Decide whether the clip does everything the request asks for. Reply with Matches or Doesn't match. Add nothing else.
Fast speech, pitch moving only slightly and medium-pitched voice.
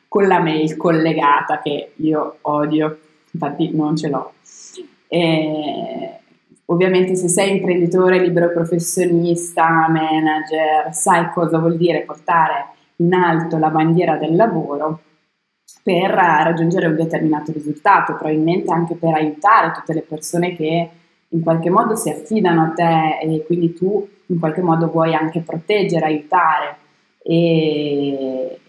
Doesn't match